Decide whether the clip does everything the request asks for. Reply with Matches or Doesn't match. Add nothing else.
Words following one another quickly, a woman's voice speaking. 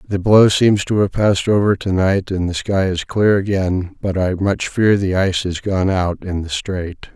Doesn't match